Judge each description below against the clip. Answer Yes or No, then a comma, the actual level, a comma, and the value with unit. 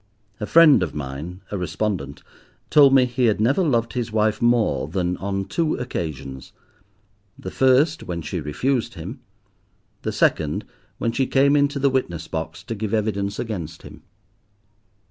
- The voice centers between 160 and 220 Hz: No, low, 105 Hz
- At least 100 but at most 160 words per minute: Yes, average, 150 wpm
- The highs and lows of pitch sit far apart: Yes, wide, 6.4 semitones